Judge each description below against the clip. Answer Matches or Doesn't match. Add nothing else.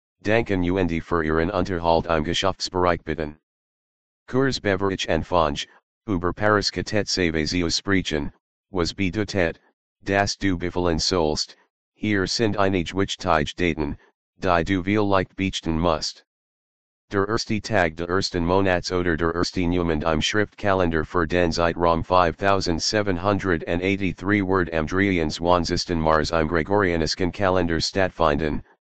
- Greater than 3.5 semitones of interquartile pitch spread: Doesn't match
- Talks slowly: Matches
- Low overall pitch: Matches